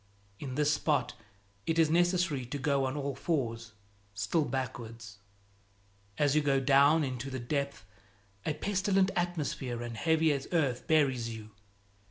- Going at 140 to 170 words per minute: Yes, average, 145 wpm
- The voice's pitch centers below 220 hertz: Yes, medium, 140 Hz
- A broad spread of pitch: No, average, 4.3 semitones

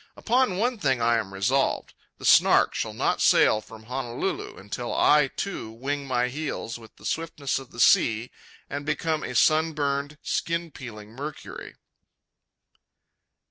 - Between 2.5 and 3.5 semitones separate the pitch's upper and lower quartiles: No, average, 4.8 semitones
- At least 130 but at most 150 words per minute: Yes, average, 145 wpm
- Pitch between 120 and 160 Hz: Yes, low, 135 Hz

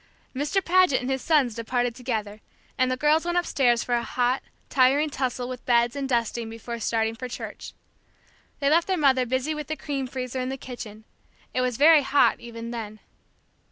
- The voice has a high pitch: Yes, very high, 255 Hz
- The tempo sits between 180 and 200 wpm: Yes, average, 190 wpm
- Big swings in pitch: No, average, 3.1 semitones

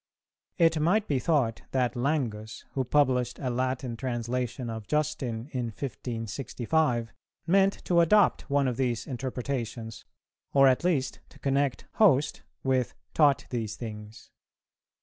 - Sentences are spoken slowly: Yes, slow, 130 wpm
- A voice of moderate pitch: No, low, 130 Hz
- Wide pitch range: No, average, 3.5 semitones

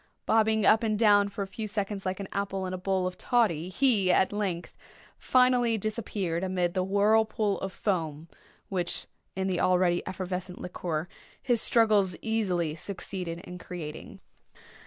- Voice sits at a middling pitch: No, high, 195 Hz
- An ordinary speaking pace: Yes, average, 155 wpm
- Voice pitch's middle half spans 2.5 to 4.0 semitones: Yes, average, 3.1 semitones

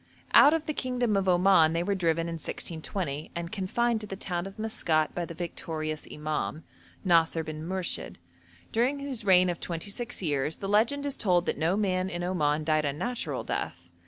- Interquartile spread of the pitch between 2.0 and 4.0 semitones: No, average, 4.6 semitones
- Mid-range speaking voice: Yes, medium, 175 Hz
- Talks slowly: No, average, 190 wpm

